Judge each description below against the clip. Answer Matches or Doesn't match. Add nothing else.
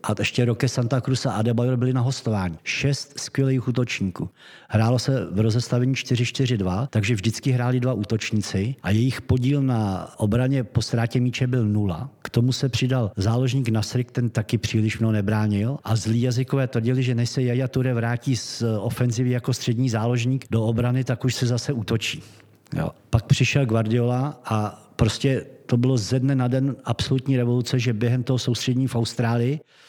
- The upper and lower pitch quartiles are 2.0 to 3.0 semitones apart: Matches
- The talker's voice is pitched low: Matches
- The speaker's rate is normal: Doesn't match